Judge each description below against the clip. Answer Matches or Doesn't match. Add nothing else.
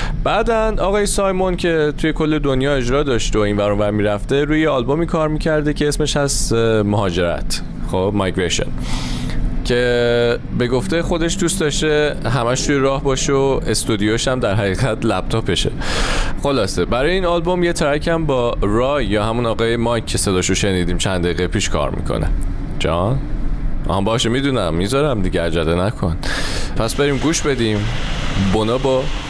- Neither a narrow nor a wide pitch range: Doesn't match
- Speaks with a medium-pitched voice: Doesn't match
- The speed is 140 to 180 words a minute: Matches